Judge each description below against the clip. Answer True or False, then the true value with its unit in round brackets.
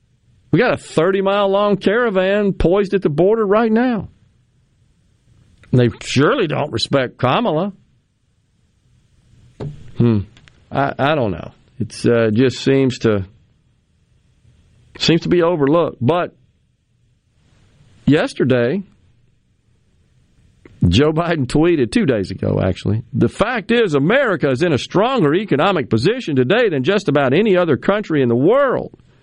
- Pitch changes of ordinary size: False (8.0 semitones)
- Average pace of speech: False (125 wpm)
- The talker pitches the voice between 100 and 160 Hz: True (135 Hz)